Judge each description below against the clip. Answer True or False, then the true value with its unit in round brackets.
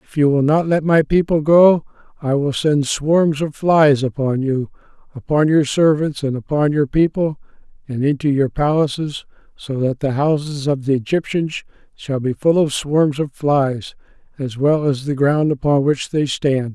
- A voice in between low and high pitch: True (145 Hz)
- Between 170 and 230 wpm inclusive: True (180 wpm)